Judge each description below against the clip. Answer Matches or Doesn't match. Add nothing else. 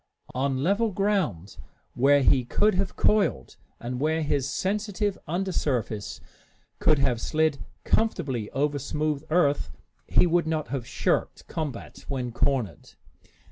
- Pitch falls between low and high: Matches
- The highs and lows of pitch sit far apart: Matches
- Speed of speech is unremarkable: Doesn't match